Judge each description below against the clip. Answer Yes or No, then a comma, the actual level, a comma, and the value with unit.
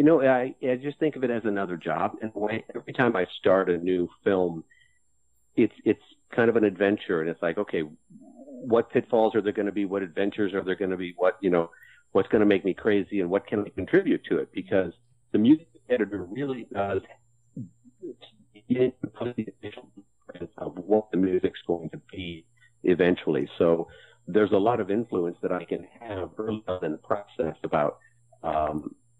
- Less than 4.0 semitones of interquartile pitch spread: No, average, 5.1 semitones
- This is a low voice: Yes, low, 110 Hz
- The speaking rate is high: No, average, 190 wpm